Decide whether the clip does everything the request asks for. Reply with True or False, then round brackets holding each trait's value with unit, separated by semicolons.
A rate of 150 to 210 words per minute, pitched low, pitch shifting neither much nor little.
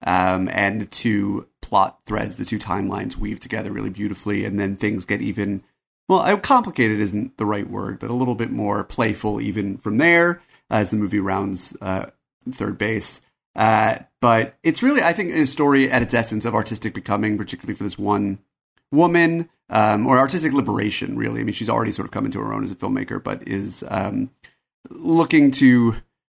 True (185 wpm; 105 Hz; 4.6 semitones)